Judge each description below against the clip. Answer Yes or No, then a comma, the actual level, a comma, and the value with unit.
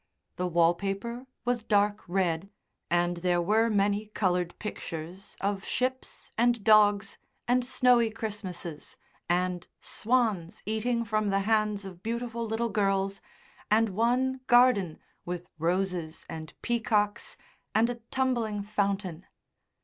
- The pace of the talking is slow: Yes, slow, 120 wpm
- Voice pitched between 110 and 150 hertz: No, high, 205 Hz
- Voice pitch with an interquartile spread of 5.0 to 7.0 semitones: No, average, 4.0 semitones